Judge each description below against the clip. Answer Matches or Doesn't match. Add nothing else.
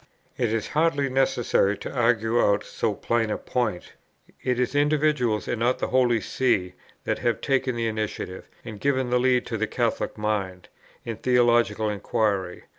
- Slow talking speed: Doesn't match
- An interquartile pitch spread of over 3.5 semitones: Doesn't match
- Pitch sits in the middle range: Doesn't match